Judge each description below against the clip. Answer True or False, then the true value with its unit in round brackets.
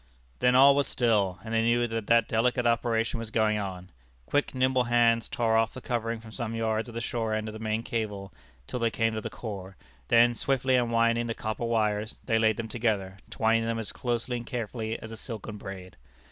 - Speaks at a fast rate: True (215 wpm)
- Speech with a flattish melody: True (1.5 semitones)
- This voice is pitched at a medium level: False (115 Hz)